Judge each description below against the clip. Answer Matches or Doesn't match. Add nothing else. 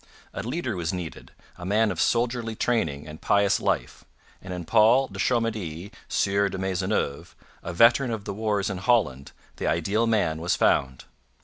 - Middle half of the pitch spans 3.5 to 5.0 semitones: Matches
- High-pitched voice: Doesn't match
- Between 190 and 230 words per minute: Doesn't match